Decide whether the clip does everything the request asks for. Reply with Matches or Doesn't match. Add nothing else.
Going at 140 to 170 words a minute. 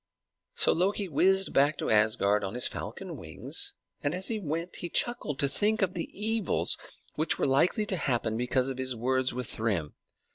Doesn't match